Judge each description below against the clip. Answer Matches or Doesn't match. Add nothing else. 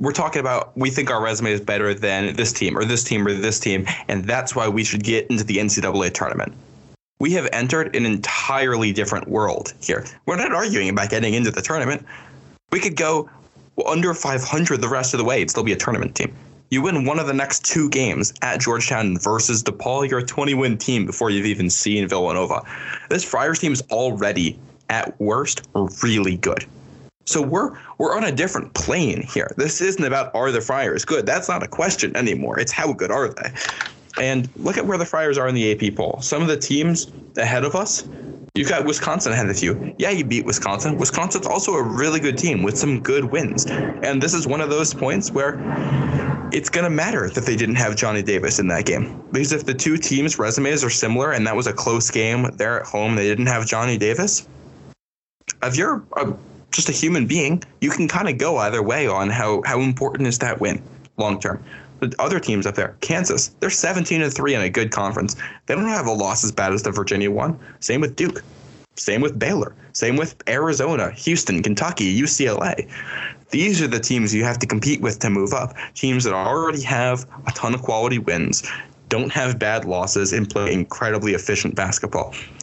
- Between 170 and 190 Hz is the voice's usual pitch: Doesn't match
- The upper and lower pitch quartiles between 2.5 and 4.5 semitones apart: Doesn't match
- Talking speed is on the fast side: Matches